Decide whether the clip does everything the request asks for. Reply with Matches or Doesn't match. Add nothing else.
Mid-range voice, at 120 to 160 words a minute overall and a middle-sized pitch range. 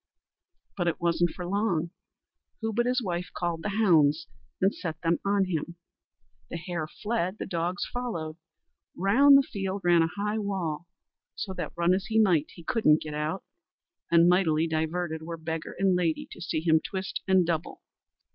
Doesn't match